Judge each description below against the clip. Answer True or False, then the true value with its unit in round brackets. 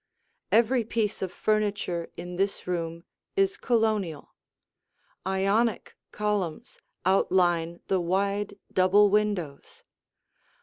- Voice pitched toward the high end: True (195 Hz)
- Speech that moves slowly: True (90 wpm)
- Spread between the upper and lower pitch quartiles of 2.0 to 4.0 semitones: True (3.1 semitones)